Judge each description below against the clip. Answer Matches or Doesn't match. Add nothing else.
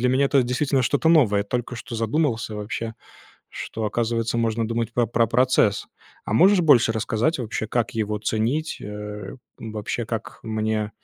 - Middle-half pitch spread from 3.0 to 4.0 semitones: Doesn't match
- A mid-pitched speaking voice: Doesn't match